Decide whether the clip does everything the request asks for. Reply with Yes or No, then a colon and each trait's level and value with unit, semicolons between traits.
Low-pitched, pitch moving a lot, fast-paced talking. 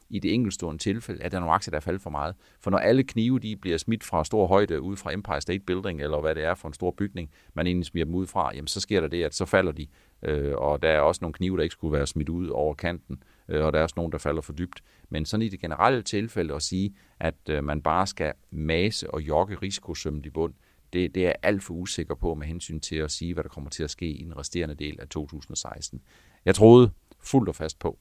No: very low, 85 Hz; average, 3.7 semitones; fast, 265 wpm